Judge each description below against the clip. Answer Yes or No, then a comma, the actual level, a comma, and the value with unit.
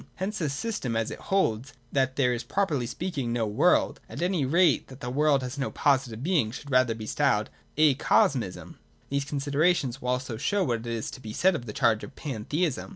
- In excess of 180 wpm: Yes, average, 200 wpm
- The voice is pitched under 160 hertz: Yes, low, 135 Hz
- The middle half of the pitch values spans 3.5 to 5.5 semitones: Yes, average, 4.4 semitones